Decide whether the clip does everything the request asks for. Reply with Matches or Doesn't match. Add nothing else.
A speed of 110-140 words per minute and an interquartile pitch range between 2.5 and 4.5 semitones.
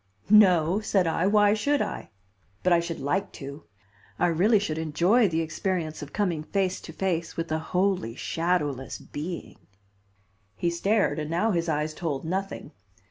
Doesn't match